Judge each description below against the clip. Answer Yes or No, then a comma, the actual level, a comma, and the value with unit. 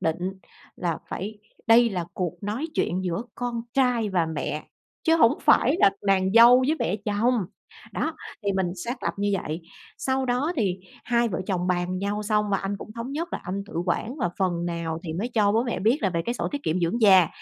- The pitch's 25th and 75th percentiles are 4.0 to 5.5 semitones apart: Yes, average, 4.8 semitones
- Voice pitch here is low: No, high, 205 Hz